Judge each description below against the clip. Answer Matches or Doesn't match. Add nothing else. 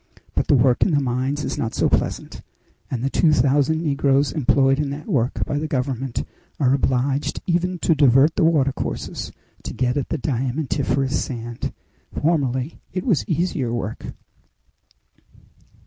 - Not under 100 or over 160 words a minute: Matches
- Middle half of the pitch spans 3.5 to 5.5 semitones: Doesn't match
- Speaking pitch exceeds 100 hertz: Matches